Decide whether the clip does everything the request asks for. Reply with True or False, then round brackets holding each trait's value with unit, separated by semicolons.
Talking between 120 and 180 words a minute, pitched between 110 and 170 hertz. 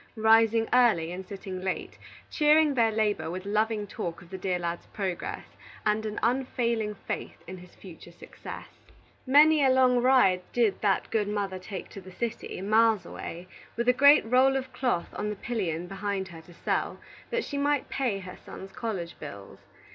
False (175 wpm; 210 Hz)